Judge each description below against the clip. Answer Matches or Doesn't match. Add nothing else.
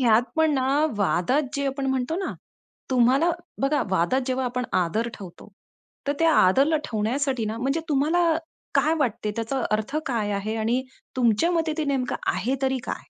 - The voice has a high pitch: Matches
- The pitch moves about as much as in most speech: Matches